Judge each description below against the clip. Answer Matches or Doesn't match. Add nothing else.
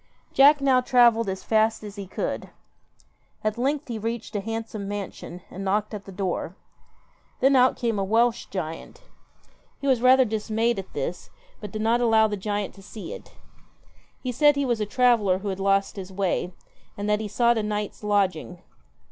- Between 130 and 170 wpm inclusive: Doesn't match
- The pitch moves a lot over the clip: Doesn't match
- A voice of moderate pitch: Doesn't match